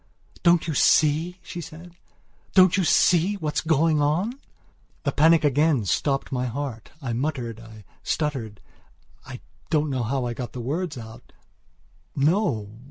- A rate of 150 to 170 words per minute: No, average, 140 wpm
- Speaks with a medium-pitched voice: Yes, medium, 145 Hz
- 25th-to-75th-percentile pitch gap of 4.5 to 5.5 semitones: Yes, average, 5.1 semitones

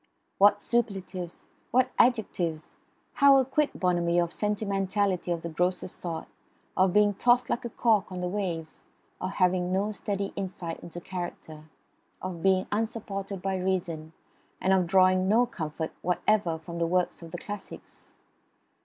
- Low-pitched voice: No, medium, 185 Hz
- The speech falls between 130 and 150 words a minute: Yes, average, 145 wpm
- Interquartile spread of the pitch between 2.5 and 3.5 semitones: Yes, average, 2.9 semitones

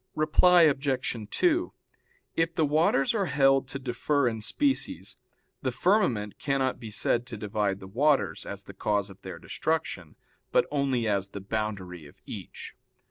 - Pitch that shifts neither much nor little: No, wide, 6.7 semitones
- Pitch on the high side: No, low, 125 Hz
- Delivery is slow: No, average, 155 wpm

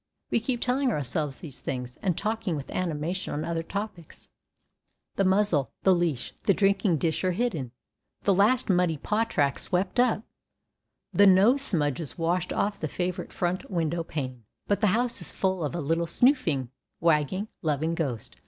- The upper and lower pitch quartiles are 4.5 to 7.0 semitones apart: Yes, average, 4.9 semitones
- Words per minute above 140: Yes, average, 165 wpm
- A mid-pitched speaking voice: Yes, medium, 175 Hz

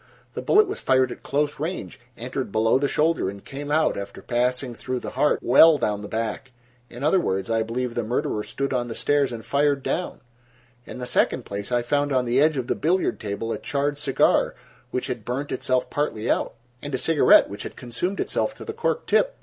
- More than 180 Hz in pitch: No, low, 130 Hz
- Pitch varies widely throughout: No, average, 3.8 semitones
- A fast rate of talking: Yes, fast, 215 wpm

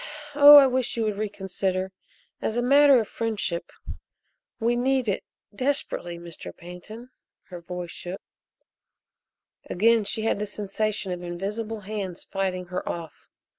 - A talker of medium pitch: No, high, 205 Hz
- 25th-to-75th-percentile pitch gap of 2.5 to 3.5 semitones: No, average, 4.2 semitones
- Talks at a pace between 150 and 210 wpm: No, slow, 135 wpm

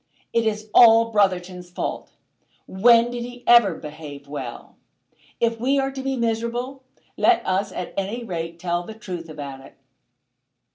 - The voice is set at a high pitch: Yes, high, 210 Hz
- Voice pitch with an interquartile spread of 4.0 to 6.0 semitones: Yes, wide, 5.5 semitones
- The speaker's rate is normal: Yes, average, 150 wpm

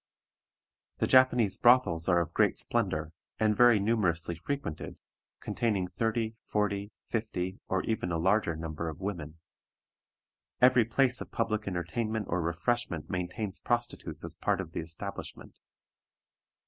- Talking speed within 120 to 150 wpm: Yes, slow, 135 wpm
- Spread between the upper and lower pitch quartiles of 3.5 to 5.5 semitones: Yes, average, 5.1 semitones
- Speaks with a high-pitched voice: No, low, 100 Hz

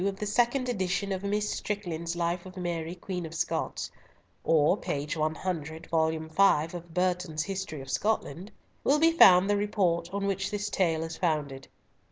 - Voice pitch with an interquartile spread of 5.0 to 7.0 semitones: No, average, 3.6 semitones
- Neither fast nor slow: Yes, average, 170 wpm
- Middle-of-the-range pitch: Yes, medium, 180 Hz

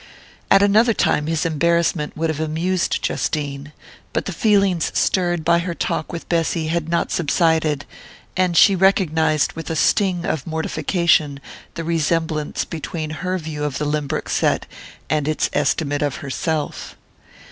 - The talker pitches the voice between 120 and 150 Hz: No, medium, 160 Hz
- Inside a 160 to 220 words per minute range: No, average, 145 wpm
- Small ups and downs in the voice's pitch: Yes, narrow, 2.2 semitones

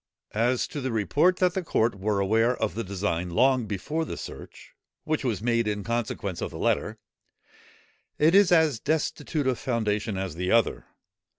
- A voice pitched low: Yes, low, 115 Hz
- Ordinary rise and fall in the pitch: No, wide, 6.1 semitones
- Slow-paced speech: No, average, 175 wpm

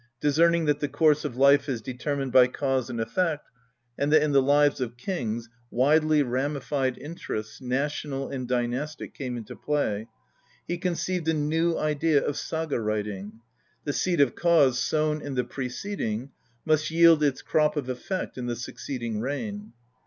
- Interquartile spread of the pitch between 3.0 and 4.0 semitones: Yes, average, 3.7 semitones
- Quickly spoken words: No, average, 160 wpm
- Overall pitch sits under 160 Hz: Yes, medium, 140 Hz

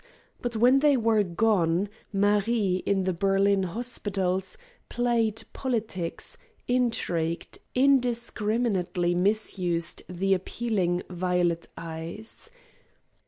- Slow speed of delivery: Yes, slow, 85 wpm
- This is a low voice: No, high, 200 Hz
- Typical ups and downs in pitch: Yes, average, 4.4 semitones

